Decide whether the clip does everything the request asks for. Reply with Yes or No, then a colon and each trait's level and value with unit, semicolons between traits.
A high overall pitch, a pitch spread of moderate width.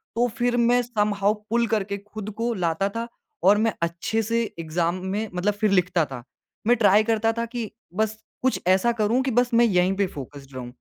Yes: high, 210 Hz; average, 3.9 semitones